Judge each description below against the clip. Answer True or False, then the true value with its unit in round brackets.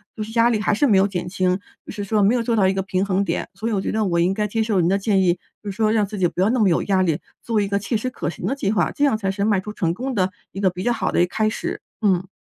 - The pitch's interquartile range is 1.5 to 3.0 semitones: True (2.6 semitones)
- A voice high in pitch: True (200 Hz)